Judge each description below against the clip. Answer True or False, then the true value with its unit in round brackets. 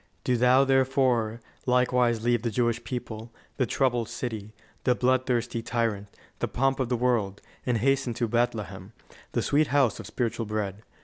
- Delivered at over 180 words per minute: False (160 wpm)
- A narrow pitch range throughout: True (2.1 semitones)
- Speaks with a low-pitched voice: True (120 Hz)